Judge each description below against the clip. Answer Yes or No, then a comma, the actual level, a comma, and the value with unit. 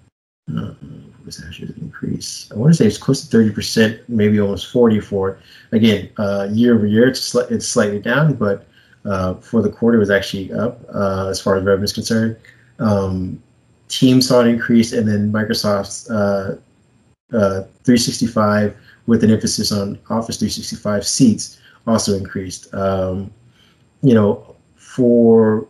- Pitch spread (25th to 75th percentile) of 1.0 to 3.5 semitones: Yes, average, 2.8 semitones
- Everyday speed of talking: Yes, average, 155 wpm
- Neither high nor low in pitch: No, low, 105 Hz